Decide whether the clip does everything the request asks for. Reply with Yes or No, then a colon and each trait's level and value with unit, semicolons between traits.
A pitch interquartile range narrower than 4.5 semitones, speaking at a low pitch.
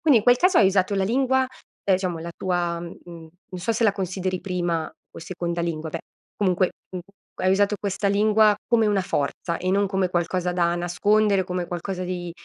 No: average, 2.7 semitones; medium, 185 Hz